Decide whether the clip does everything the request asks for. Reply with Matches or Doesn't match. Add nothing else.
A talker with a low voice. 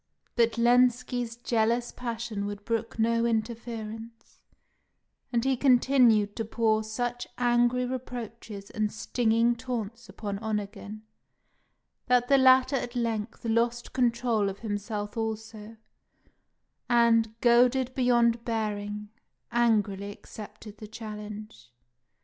Doesn't match